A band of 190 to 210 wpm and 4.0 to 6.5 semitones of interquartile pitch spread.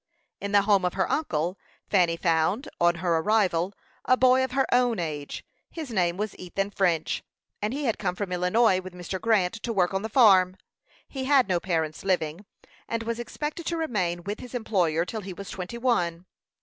Yes: average, 195 wpm; average, 4.6 semitones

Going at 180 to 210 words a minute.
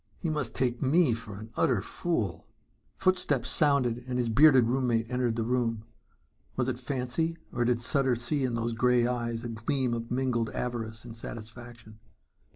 No: average, 165 wpm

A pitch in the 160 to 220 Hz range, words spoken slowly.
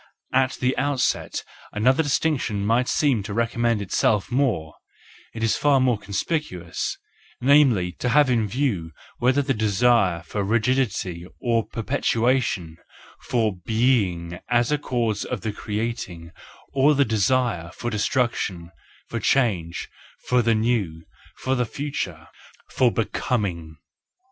No: low, 115 Hz; slow, 120 wpm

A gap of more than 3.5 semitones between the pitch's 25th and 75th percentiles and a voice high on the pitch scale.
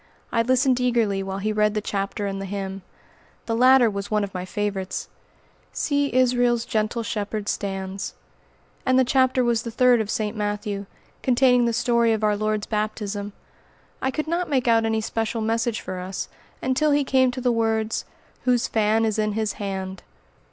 No: average, 3.2 semitones; high, 220 Hz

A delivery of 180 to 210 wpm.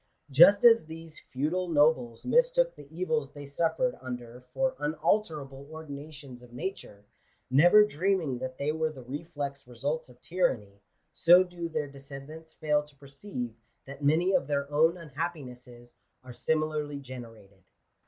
No: average, 140 wpm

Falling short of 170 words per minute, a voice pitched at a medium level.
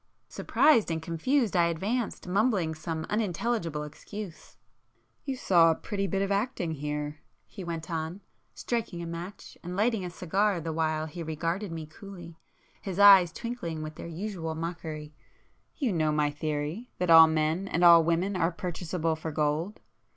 Yes: average, 160 wpm; medium, 170 Hz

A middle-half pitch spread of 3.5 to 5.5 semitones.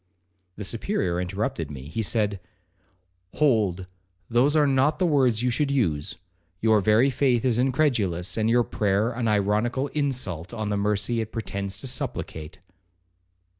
Yes: average, 4.6 semitones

